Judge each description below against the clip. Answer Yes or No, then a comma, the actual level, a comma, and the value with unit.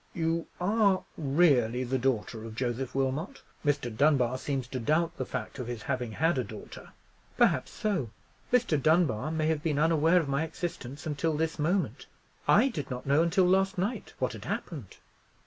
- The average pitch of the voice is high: No, medium, 150 Hz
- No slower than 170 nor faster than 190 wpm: Yes, average, 175 wpm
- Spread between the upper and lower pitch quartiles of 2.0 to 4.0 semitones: No, average, 4.7 semitones